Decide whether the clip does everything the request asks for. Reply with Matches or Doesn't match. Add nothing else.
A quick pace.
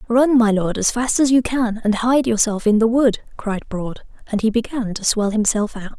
Matches